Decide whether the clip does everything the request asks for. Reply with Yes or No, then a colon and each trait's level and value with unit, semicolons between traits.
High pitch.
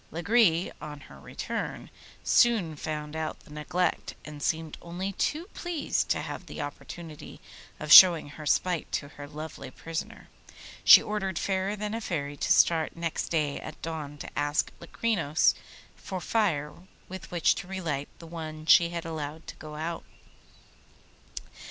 No: medium, 165 Hz